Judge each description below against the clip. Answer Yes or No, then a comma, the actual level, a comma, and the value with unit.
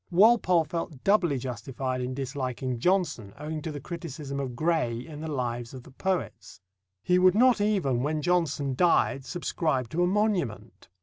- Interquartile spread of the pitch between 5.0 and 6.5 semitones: Yes, wide, 5.6 semitones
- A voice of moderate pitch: Yes, medium, 150 Hz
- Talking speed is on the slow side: No, average, 165 wpm